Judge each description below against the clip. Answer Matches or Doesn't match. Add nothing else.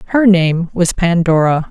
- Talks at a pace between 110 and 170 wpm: Matches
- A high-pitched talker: Doesn't match